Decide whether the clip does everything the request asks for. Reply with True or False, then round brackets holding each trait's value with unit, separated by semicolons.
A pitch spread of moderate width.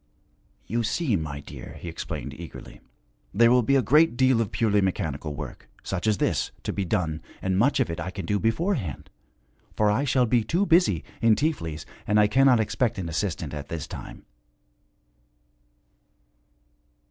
False (6.9 semitones)